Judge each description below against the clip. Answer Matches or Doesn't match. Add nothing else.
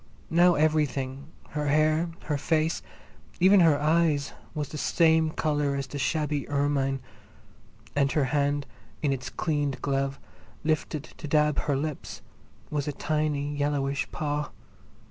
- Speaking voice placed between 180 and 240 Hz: Doesn't match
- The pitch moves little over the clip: Matches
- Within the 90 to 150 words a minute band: Matches